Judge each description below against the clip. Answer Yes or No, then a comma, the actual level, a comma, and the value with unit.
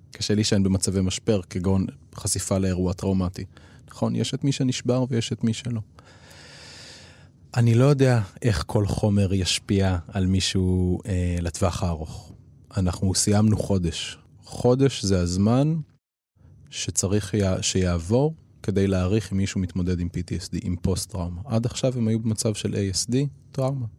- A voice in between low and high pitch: No, low, 100 Hz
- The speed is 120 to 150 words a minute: Yes, average, 140 wpm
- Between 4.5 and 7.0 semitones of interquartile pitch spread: No, average, 3.9 semitones